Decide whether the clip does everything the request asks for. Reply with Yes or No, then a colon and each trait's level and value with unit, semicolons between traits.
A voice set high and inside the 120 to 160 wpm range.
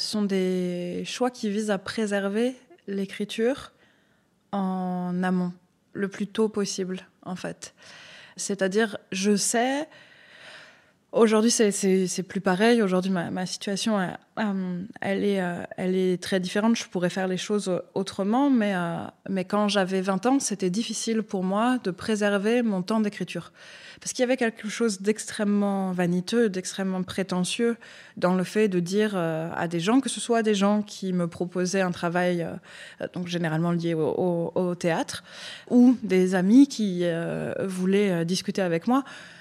Yes: high, 195 Hz; average, 155 wpm